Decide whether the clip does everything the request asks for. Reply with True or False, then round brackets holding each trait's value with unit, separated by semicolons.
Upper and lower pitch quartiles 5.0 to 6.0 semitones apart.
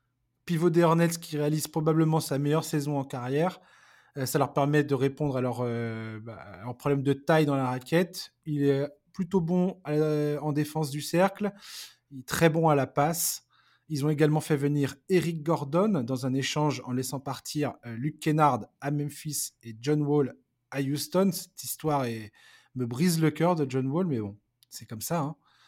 False (3.4 semitones)